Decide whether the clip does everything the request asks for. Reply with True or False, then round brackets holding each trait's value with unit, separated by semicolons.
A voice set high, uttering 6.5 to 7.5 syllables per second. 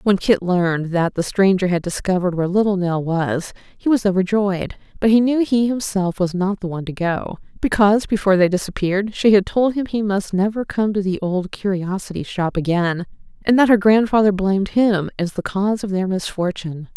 False (195 Hz; 5.5 syllables/s)